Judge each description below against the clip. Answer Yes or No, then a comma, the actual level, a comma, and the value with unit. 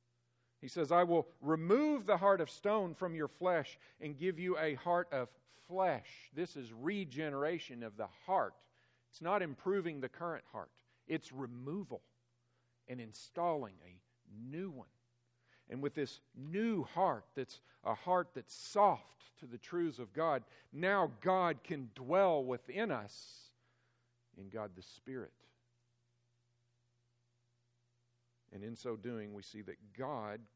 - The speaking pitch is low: Yes, low, 130 Hz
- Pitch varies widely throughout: Yes, wide, 6.0 semitones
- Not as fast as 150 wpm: Yes, average, 140 wpm